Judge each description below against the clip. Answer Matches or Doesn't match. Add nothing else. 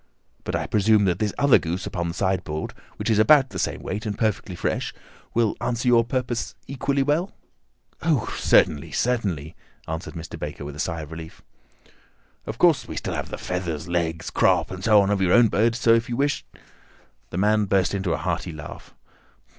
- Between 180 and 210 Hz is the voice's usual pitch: Doesn't match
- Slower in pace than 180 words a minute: Doesn't match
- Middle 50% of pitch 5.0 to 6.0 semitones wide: Matches